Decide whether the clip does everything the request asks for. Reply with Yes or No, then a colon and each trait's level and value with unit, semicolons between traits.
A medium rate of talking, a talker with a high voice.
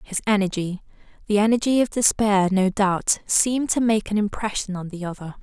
Yes: average, 165 wpm; high, 205 Hz